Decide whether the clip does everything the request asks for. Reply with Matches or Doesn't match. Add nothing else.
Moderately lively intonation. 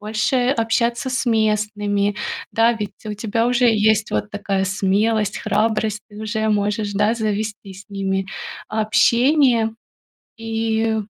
Doesn't match